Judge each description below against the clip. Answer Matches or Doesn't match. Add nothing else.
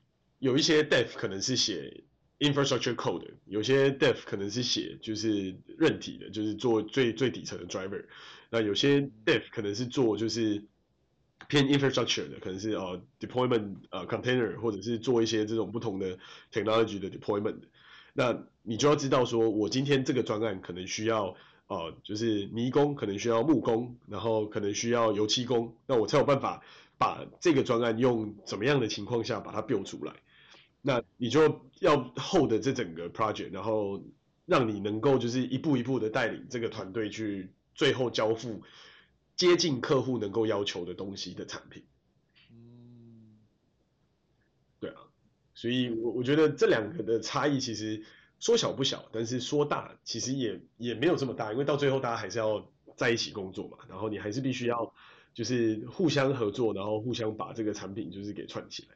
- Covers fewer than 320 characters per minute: Doesn't match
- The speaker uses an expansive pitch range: Doesn't match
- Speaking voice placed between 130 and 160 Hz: Doesn't match